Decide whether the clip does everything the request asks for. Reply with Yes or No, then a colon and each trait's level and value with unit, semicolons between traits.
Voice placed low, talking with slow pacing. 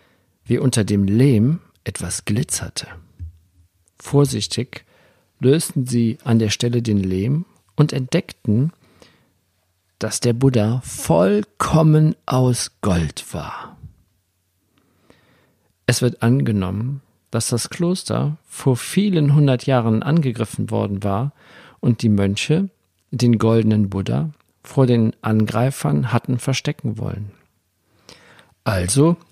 Yes: low, 115 Hz; slow, 100 wpm